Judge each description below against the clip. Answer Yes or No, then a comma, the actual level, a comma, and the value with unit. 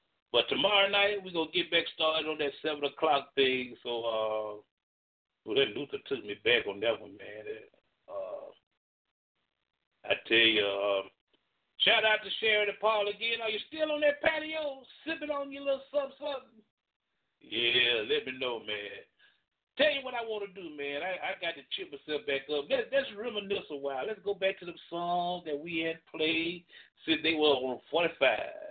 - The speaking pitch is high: Yes, high, 200 Hz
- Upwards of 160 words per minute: Yes, average, 190 wpm